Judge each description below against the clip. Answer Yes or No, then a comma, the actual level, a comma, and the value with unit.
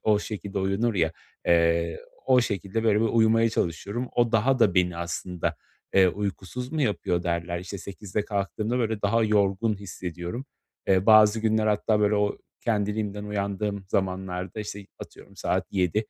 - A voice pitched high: No, low, 105 Hz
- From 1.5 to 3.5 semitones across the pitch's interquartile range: Yes, average, 2.9 semitones